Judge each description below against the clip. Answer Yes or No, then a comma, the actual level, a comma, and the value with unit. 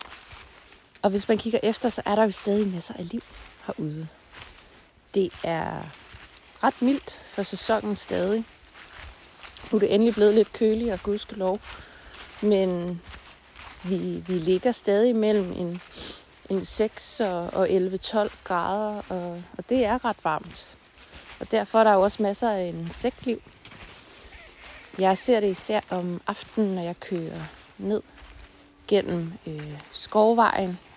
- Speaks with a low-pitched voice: No, high, 200 Hz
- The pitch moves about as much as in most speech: Yes, average, 3.4 semitones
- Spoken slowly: Yes, slow, 140 wpm